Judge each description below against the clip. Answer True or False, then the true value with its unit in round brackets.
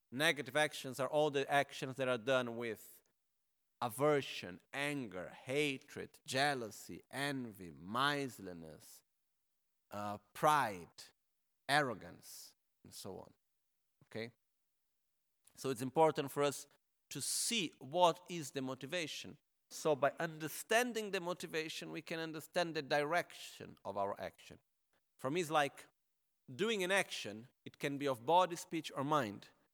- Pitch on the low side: False (145 Hz)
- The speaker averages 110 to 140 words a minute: True (125 wpm)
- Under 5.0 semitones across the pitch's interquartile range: True (3.6 semitones)